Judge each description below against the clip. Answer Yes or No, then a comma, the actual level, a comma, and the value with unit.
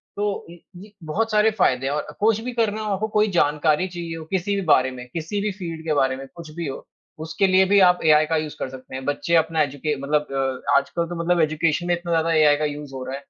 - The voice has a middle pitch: Yes, medium, 160 Hz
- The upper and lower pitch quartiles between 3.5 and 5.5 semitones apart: Yes, average, 4.2 semitones